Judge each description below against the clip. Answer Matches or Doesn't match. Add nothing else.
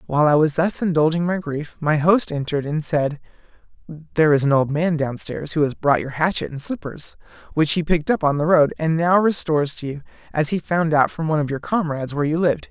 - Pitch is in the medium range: Matches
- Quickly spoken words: Matches